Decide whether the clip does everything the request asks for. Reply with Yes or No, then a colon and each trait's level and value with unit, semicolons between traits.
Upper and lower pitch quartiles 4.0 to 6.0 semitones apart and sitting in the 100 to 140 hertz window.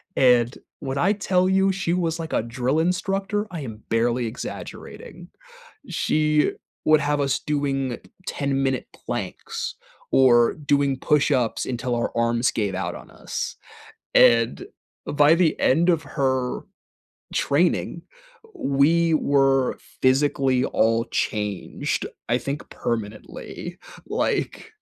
Yes: average, 4.7 semitones; low, 135 Hz